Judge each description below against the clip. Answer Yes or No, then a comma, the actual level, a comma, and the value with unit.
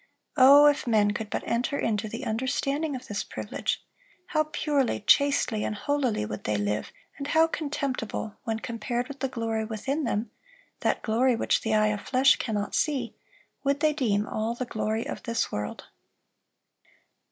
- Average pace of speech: Yes, average, 160 wpm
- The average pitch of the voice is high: Yes, high, 235 Hz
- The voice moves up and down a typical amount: Yes, average, 4.5 semitones